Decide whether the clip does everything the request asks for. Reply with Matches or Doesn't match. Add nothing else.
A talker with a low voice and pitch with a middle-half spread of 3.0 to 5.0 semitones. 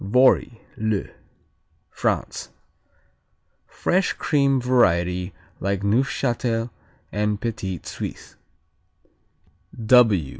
Matches